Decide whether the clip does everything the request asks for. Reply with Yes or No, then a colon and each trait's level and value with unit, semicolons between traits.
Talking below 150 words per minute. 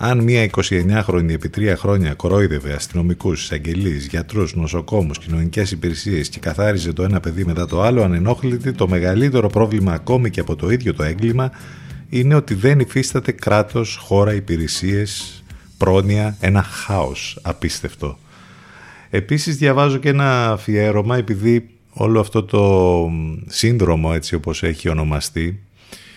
Yes: average, 130 wpm